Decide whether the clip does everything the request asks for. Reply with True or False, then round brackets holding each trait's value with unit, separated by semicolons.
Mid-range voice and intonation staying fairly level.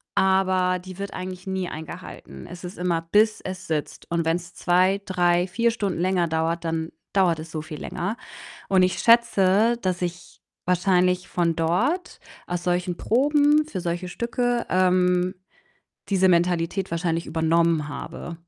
True (180 Hz; 2.1 semitones)